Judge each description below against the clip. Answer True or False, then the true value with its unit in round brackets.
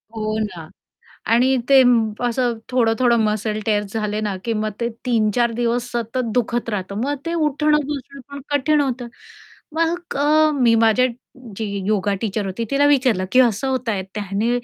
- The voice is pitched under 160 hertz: False (235 Hz)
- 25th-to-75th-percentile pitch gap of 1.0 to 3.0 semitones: False (3.6 semitones)